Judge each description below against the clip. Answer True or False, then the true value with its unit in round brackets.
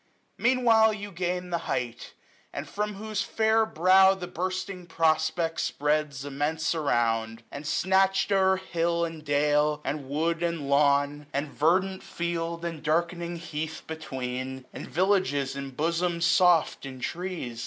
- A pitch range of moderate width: True (4.0 semitones)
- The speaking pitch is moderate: True (165 Hz)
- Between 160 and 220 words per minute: False (140 wpm)